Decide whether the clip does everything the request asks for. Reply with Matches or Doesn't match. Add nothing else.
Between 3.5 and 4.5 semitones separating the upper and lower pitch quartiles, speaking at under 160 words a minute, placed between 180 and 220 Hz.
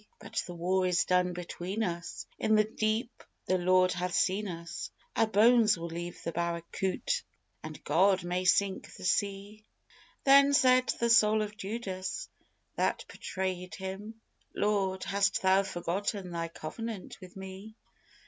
Doesn't match